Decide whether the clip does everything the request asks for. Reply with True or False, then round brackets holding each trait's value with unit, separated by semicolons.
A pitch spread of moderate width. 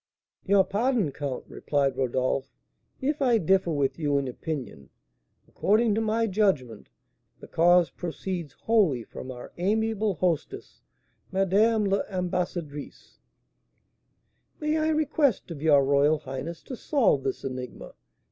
False (7.5 semitones)